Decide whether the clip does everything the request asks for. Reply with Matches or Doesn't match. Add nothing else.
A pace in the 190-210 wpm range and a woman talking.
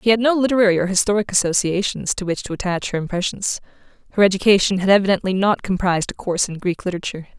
Matches